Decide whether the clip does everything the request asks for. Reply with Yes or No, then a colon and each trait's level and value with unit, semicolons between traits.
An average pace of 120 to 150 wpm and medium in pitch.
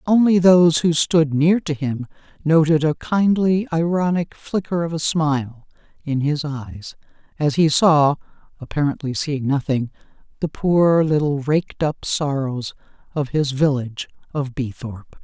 Yes: average, 140 wpm; medium, 150 Hz